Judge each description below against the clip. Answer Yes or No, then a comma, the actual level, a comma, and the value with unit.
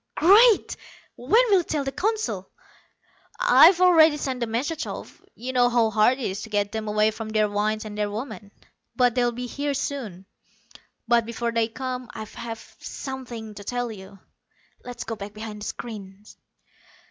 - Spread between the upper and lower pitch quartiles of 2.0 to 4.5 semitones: Yes, average, 3.8 semitones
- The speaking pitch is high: Yes, high, 235 Hz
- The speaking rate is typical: Yes, average, 170 wpm